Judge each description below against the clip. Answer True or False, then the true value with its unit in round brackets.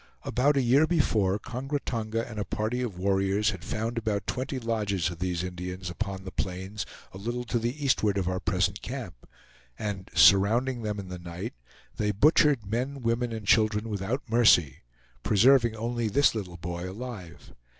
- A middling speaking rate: True (170 wpm)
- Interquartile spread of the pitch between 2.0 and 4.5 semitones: True (4.2 semitones)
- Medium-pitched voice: False (110 Hz)